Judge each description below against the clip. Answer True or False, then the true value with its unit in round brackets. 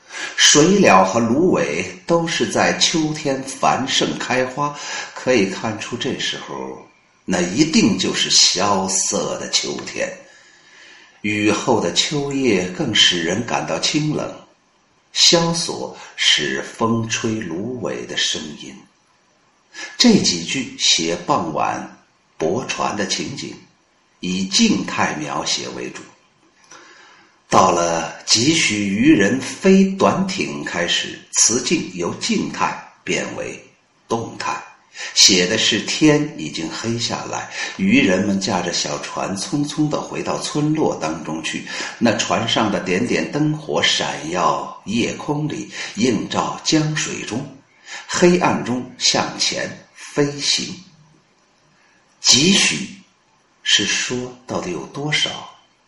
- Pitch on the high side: False (135 Hz)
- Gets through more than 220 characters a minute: False (160 characters per minute)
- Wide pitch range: True (6.9 semitones)